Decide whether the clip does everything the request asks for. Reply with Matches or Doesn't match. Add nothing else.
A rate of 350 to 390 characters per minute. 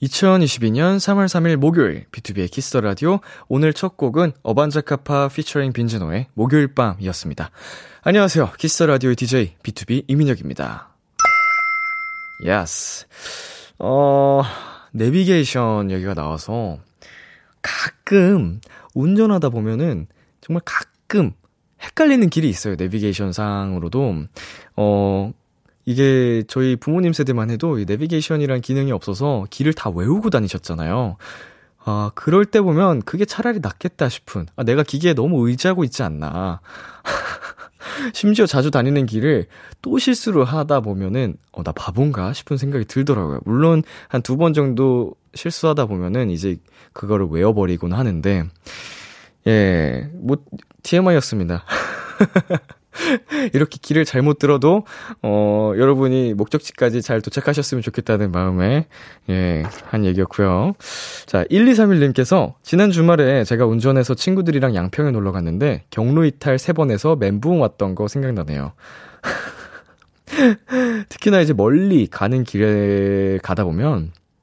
Doesn't match